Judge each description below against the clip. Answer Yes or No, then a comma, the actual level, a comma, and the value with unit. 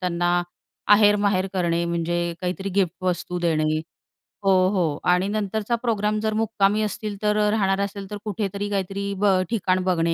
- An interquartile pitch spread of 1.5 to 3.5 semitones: Yes, average, 2.7 semitones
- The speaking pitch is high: Yes, high, 195 Hz